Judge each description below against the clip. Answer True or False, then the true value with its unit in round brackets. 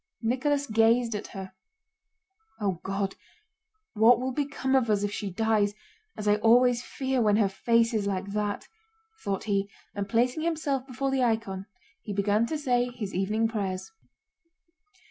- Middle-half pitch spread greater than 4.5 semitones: False (3.5 semitones)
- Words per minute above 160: False (155 wpm)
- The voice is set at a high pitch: True (225 Hz)